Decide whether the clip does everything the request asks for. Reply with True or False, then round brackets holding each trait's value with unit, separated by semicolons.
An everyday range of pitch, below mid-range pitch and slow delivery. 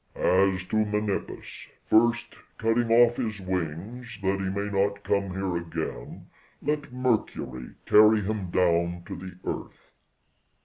True (3.4 semitones; 100 Hz; 130 wpm)